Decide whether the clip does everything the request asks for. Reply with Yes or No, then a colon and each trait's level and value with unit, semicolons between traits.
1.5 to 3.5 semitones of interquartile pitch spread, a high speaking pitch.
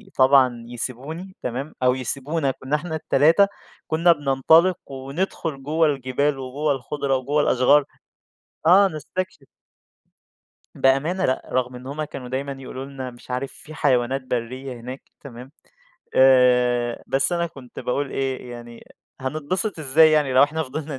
No: average, 3.2 semitones; low, 135 Hz